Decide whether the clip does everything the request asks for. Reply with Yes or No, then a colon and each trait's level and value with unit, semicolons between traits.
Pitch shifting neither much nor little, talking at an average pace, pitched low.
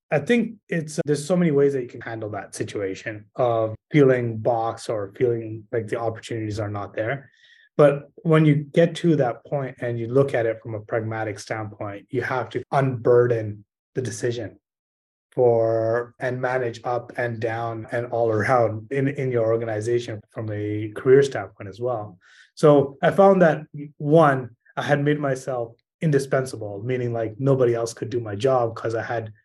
Yes: average, 3.7 semitones; average, 175 wpm; low, 120 Hz